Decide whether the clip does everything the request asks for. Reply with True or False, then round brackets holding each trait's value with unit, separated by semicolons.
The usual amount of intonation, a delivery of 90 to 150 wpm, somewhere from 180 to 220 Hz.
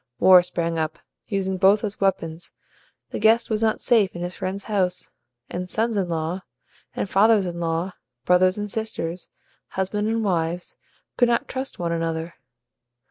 False (3.6 semitones; 160 wpm; 185 Hz)